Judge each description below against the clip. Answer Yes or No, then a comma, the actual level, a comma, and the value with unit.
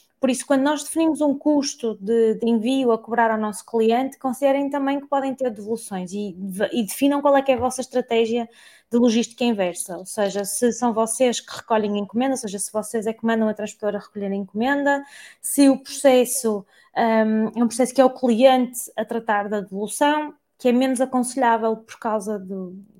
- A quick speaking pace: Yes, fast, 200 wpm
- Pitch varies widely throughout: No, average, 3.5 semitones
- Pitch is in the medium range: No, high, 235 Hz